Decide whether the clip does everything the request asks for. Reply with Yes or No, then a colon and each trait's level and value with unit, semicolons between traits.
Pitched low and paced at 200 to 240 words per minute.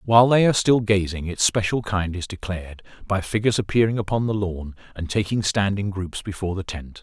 Yes: low, 100 Hz; fast, 205 wpm